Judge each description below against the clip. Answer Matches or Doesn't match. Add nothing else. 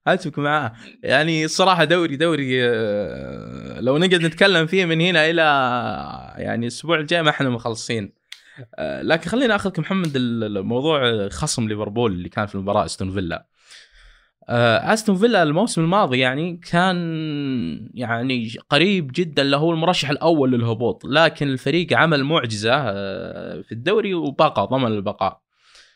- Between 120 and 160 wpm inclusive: Matches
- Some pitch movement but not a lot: Doesn't match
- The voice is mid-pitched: Matches